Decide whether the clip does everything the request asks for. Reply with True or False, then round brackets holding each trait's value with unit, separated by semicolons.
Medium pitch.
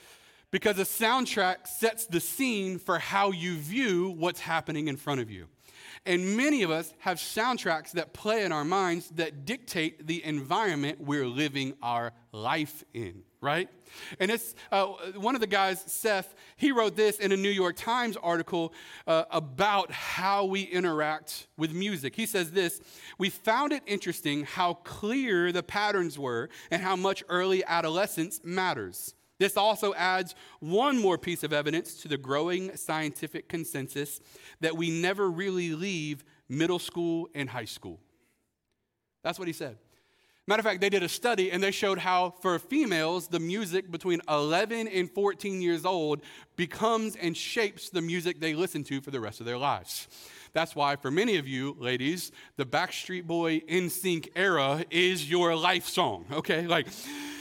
True (175 Hz)